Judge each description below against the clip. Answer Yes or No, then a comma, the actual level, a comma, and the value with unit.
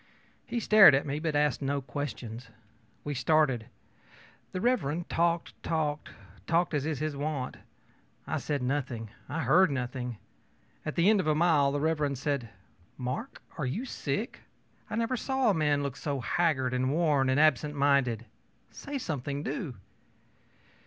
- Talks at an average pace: Yes, average, 150 wpm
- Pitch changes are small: No, average, 3.6 semitones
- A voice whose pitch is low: No, medium, 145 Hz